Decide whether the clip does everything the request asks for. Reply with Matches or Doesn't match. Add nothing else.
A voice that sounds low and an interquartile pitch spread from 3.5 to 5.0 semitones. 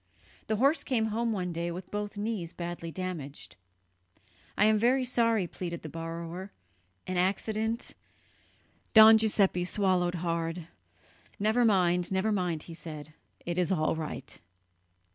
Doesn't match